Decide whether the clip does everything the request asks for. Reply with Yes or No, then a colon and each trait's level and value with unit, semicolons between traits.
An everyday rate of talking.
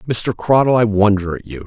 No: fast, 215 wpm